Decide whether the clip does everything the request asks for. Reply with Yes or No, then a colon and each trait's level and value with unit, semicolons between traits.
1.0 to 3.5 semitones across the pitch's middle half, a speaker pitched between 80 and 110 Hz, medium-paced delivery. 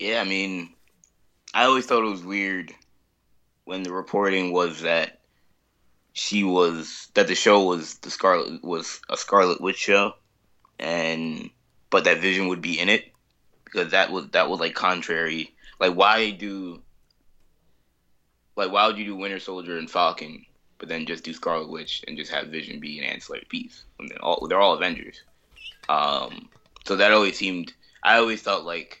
Yes: average, 3.1 semitones; very low, 95 Hz; average, 175 wpm